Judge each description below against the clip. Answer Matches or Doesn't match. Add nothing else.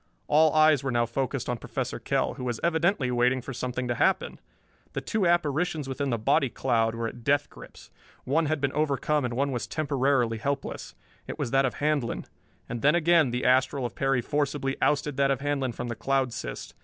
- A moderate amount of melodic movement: Matches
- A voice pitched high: Doesn't match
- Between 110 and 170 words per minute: Doesn't match